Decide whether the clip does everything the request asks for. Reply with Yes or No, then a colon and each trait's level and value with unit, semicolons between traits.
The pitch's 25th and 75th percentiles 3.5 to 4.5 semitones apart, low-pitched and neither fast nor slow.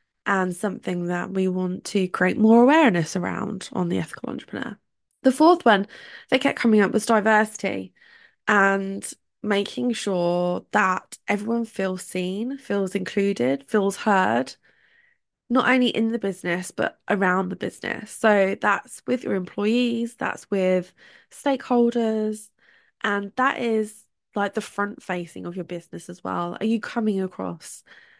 No: average, 3.8 semitones; high, 205 Hz; average, 145 wpm